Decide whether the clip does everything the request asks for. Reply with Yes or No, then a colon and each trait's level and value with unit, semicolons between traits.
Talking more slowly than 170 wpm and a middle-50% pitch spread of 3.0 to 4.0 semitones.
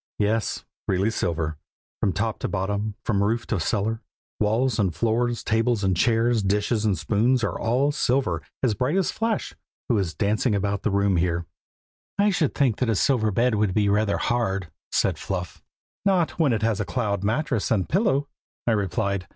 No: average, 175 wpm; average, 3.4 semitones